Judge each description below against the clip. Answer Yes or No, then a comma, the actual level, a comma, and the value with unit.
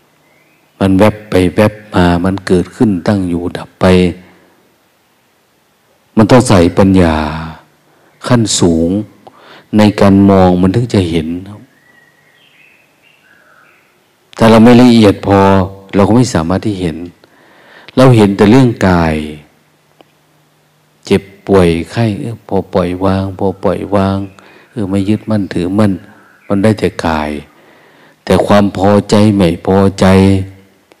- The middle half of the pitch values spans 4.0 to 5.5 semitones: No, average, 2.7 semitones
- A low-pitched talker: Yes, very low, 95 Hz